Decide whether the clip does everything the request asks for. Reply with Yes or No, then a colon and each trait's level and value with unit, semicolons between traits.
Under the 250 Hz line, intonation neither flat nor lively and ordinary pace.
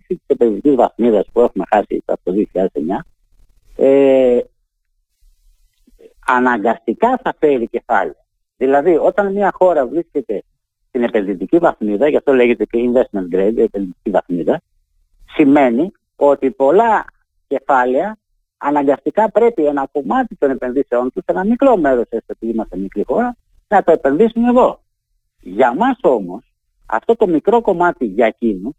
No: low, 135 Hz; wide, 8.6 semitones; average, 130 wpm